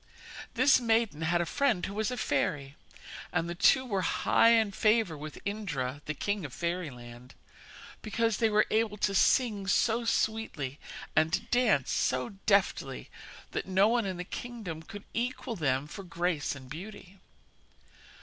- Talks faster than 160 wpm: No, average, 155 wpm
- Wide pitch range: Yes, wide, 6.2 semitones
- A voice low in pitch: No, high, 195 Hz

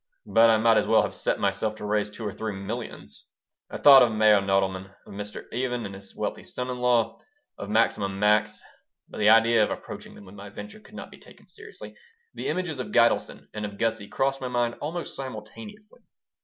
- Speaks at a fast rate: Yes, fast, 210 wpm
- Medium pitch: No, low, 110 Hz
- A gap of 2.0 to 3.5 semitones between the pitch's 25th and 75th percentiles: Yes, average, 3.2 semitones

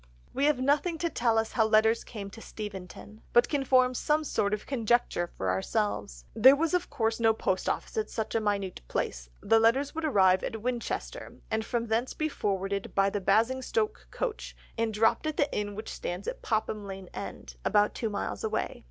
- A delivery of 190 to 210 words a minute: Yes, average, 195 wpm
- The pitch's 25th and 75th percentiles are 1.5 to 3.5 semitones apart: No, average, 4.5 semitones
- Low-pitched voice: No, high, 225 Hz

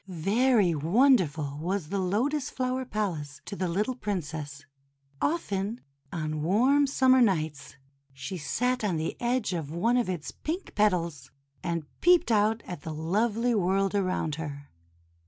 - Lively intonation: Yes, wide, 7.0 semitones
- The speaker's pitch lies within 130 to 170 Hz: No, high, 195 Hz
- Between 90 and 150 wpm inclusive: Yes, average, 140 wpm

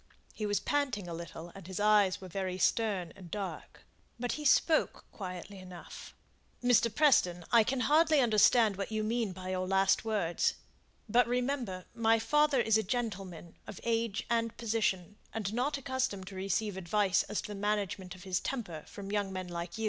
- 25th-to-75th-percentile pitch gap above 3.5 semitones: Yes, average, 3.9 semitones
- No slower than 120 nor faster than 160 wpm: No, average, 180 wpm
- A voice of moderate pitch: No, high, 205 Hz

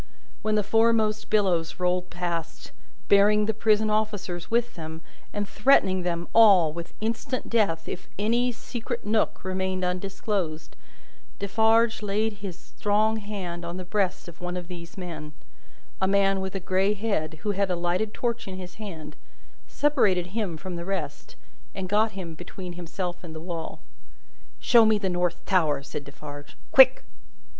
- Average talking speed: Yes, average, 160 wpm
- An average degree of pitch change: Yes, average, 3.5 semitones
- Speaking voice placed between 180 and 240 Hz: Yes, high, 190 Hz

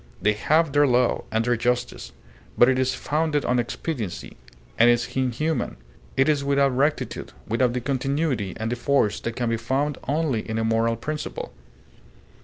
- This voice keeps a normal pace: Yes, average, 170 wpm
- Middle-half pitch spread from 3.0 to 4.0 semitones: Yes, average, 3.6 semitones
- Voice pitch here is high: No, low, 125 Hz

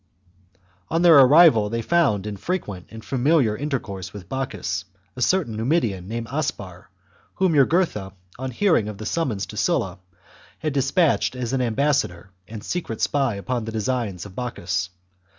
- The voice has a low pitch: Yes, low, 120 Hz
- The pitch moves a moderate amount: No, wide, 6.0 semitones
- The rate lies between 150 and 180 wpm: Yes, average, 160 wpm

